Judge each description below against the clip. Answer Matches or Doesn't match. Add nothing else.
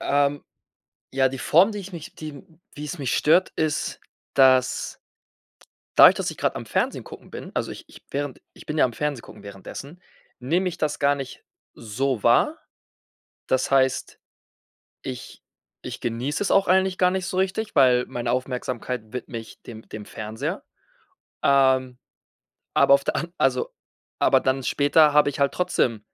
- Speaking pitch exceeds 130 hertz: Matches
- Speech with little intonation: Doesn't match